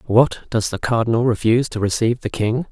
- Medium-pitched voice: No, low, 115 Hz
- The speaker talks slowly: No, average, 200 wpm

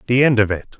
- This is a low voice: Yes, low, 115 Hz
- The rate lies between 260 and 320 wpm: Yes, fast, 300 wpm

